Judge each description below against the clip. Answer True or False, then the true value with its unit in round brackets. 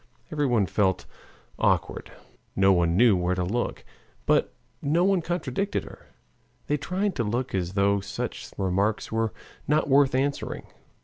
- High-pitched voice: False (115 Hz)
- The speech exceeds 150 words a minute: False (135 wpm)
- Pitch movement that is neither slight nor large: False (6.8 semitones)